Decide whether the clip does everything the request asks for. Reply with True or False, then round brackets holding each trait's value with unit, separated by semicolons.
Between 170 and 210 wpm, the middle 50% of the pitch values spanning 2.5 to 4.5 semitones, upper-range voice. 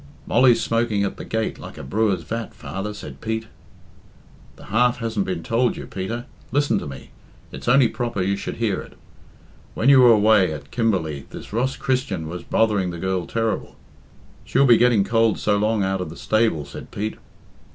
False (190 wpm; 3.7 semitones; 110 Hz)